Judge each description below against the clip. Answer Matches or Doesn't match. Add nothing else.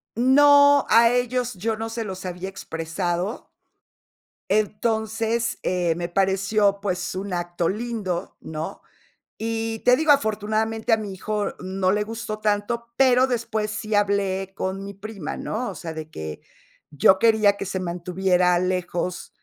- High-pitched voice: Matches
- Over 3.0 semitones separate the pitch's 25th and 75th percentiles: Matches